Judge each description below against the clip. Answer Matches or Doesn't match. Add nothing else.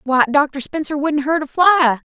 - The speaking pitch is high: Matches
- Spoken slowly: Doesn't match